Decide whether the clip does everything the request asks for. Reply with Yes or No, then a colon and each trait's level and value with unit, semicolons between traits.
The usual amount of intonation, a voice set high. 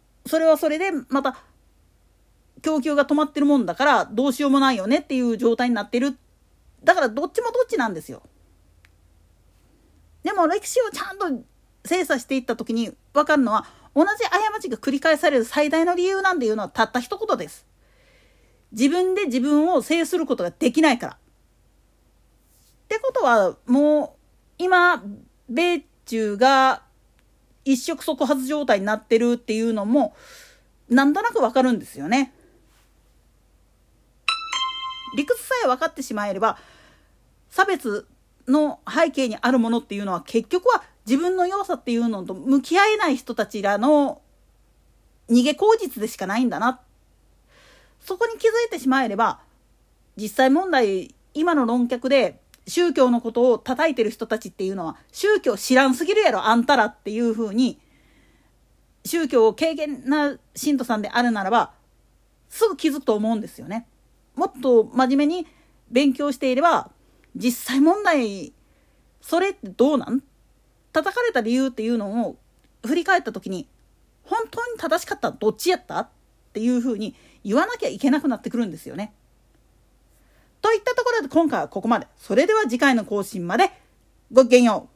No: wide, 6.5 semitones; very high, 275 Hz